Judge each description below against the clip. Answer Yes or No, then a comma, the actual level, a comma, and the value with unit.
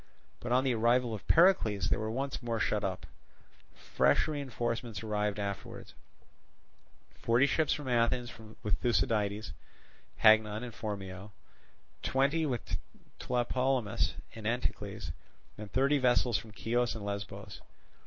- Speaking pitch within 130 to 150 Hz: No, low, 115 Hz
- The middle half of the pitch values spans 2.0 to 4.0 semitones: Yes, average, 3.2 semitones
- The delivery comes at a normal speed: No, slow, 120 wpm